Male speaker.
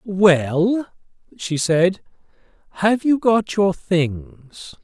Yes: male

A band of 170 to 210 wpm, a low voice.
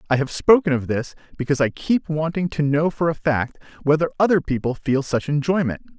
No: average, 200 wpm; medium, 150 Hz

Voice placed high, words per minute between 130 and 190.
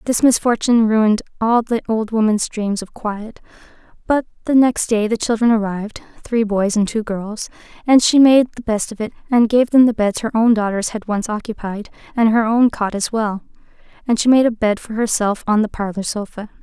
No: high, 220 Hz; average, 200 wpm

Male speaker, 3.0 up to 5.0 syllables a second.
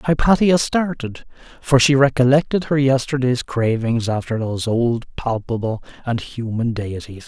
Yes: male; 4.6 syllables/s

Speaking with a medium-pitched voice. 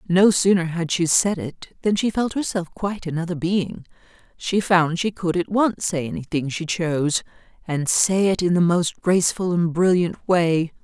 Yes: medium, 175 Hz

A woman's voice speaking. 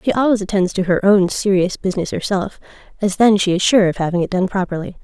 Yes: female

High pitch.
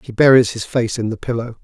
No: low, 120 Hz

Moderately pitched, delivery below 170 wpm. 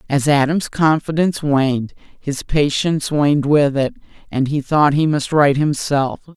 Yes: medium, 145 Hz; average, 150 wpm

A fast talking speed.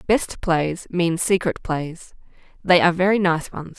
No: average, 160 wpm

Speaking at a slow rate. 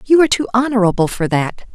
No: fast, 205 wpm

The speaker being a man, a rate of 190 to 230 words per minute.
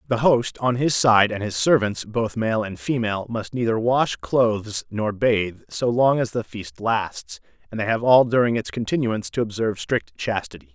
Yes: male; average, 195 wpm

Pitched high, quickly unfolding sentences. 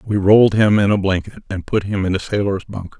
No: low, 100 Hz; fast, 260 wpm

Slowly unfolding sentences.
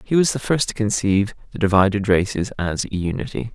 No: fast, 205 wpm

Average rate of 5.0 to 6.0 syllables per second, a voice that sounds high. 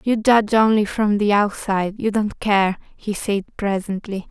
No: 4.6 syllables/s; high, 205 Hz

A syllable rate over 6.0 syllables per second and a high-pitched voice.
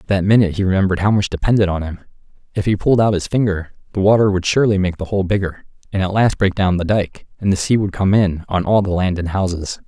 No: 6.6 syllables/s; very low, 95 Hz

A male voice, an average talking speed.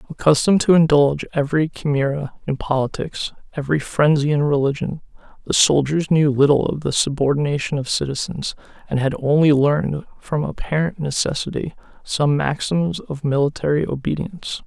No: male; slow, 130 wpm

